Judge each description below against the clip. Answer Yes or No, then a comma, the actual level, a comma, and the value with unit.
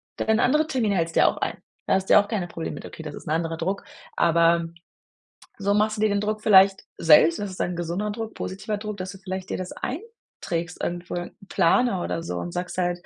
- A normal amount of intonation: Yes, average, 3.7 semitones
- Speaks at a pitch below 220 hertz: Yes, high, 190 Hz